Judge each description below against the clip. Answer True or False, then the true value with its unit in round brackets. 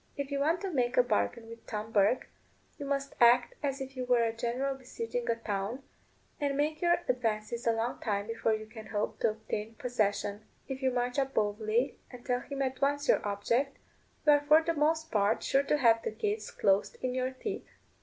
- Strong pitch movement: False (4.1 semitones)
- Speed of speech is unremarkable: False (210 wpm)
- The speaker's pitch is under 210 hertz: False (245 Hz)